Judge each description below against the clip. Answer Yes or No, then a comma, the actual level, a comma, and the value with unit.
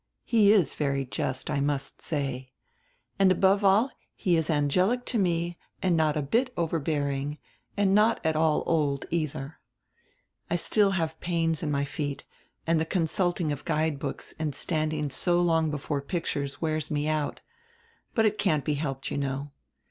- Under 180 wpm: Yes, average, 165 wpm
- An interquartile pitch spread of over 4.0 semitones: No, average, 3.5 semitones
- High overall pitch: No, medium, 155 Hz